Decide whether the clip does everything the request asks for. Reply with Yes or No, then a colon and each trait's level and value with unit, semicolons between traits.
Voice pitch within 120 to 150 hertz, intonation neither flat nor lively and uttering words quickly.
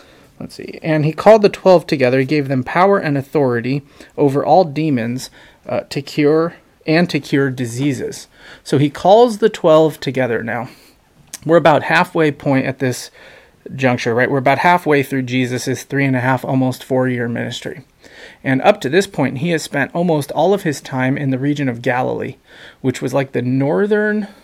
No: medium, 140 Hz; average, 3.5 semitones; average, 185 wpm